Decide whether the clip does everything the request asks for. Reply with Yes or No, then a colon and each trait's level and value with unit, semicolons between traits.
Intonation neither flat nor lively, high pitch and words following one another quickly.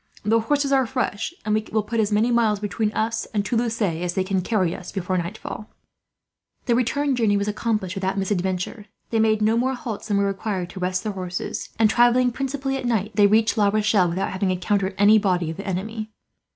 Yes: average, 3.1 semitones; high, 210 Hz; fast, 210 wpm